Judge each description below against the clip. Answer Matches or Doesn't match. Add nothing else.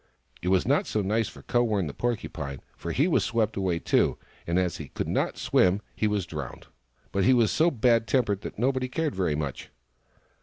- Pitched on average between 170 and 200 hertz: Doesn't match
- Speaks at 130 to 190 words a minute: Doesn't match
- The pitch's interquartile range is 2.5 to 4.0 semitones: Doesn't match